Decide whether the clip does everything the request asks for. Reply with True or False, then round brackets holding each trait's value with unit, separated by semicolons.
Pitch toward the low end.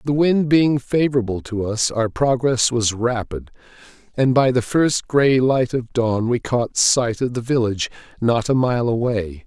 True (125 Hz)